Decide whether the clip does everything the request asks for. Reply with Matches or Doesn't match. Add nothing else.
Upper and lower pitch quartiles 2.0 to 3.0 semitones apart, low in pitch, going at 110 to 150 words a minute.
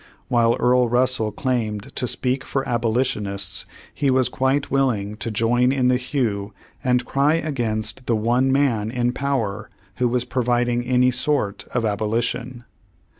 Matches